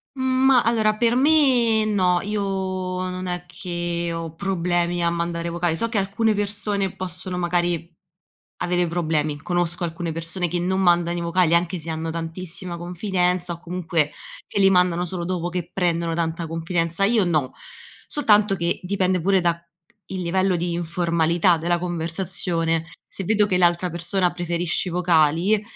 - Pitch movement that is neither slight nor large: No, narrow, 2.1 semitones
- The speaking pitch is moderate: Yes, medium, 175 Hz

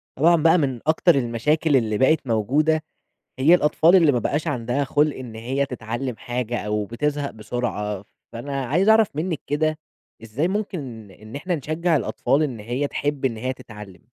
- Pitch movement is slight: No, average, 5.0 semitones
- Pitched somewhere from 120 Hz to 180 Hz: Yes, low, 135 Hz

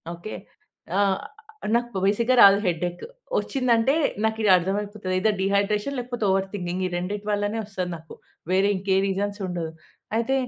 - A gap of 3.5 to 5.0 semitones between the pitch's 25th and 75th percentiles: No, average, 3.0 semitones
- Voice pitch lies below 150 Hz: No, high, 200 Hz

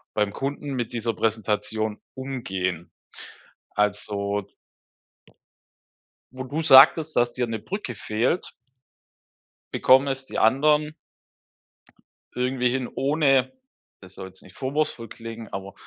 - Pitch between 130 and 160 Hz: No, low, 120 Hz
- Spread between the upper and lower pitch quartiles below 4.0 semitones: No, average, 4.4 semitones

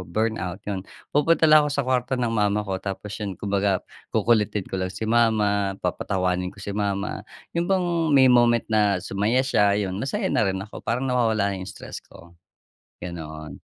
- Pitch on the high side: No, low, 105 Hz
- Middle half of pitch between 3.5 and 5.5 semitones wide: Yes, average, 3.8 semitones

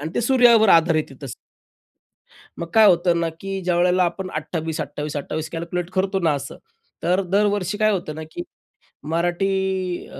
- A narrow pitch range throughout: No, average, 3.3 semitones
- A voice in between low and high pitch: Yes, medium, 175 Hz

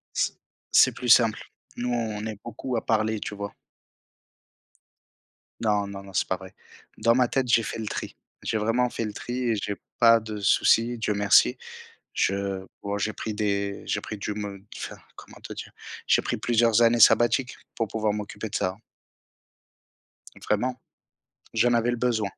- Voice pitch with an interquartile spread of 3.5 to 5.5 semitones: No, narrow, 2.5 semitones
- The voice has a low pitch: Yes, low, 110 Hz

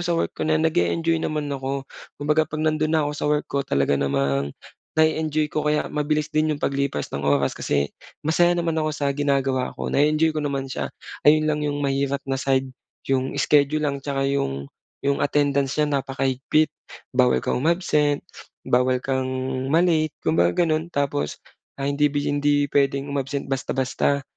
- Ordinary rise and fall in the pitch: No, narrow, 2.3 semitones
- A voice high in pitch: No, medium, 145 Hz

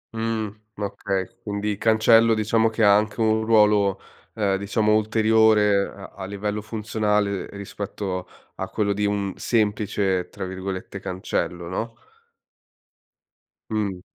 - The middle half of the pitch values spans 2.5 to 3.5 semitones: No, narrow, 1.9 semitones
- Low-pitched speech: Yes, low, 105 Hz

